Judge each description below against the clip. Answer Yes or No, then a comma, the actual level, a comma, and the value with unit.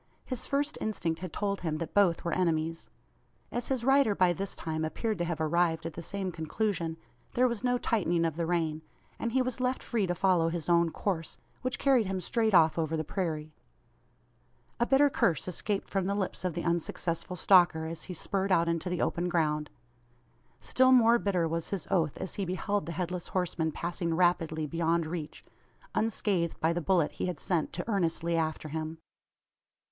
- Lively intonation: No, average, 3.6 semitones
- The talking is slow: No, average, 190 wpm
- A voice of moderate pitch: Yes, medium, 175 Hz